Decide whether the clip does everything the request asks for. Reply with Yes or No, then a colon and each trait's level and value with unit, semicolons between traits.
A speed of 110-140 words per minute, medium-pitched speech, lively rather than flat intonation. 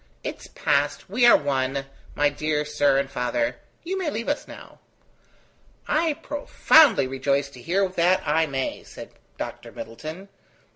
No: average, 150 wpm; medium, 150 Hz; wide, 6.4 semitones